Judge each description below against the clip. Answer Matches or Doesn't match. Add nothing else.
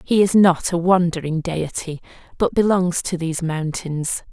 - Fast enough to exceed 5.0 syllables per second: Doesn't match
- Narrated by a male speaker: Doesn't match